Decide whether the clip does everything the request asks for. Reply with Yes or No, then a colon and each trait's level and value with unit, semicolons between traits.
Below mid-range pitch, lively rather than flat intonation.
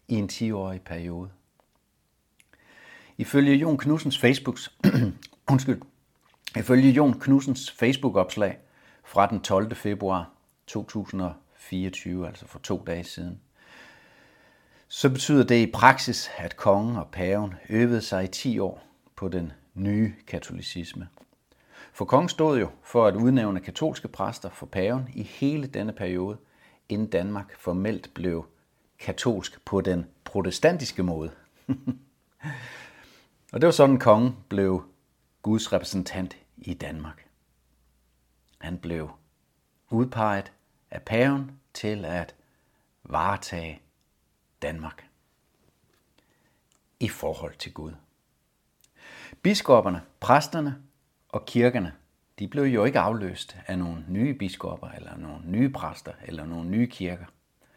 Yes: low, 100 Hz; wide, 6.5 semitones